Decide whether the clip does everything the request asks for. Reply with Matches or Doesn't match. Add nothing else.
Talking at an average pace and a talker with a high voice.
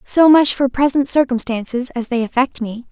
Matches